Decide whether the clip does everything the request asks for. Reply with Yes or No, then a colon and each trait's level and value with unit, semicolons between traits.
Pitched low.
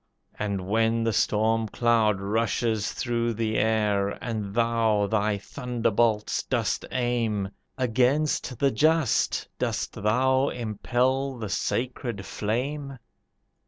Yes: low, 115 Hz